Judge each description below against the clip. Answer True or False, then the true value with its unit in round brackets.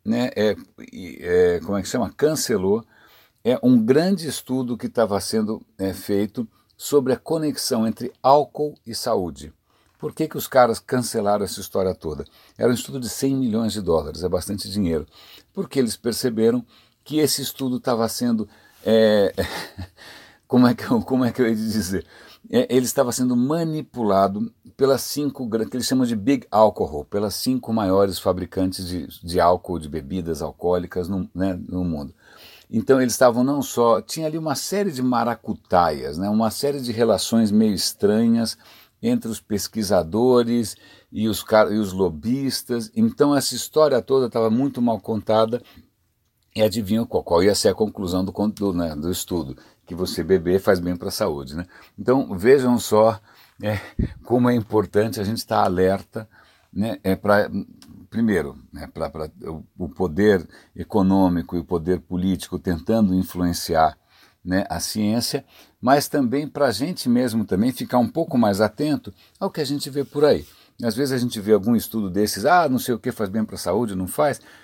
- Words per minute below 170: False (175 wpm)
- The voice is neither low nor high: False (110 Hz)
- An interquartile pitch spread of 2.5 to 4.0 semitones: False (4.8 semitones)